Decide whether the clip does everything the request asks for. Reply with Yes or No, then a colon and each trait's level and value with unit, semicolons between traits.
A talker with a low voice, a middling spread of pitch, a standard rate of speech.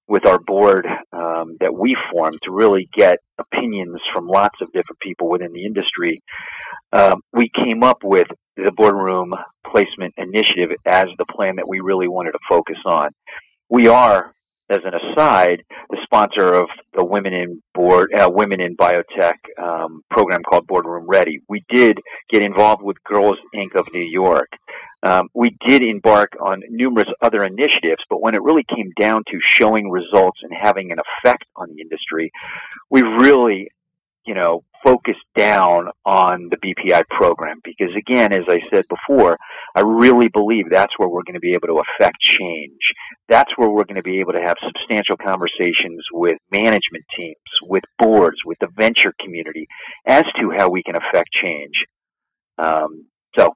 Yes: very low, 95 Hz; average, 3.7 semitones; average, 170 wpm